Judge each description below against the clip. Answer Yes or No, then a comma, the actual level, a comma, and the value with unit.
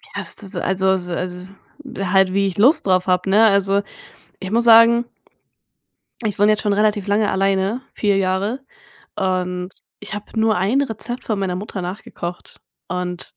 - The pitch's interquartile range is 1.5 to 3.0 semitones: Yes, narrow, 2.6 semitones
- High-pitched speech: Yes, high, 195 Hz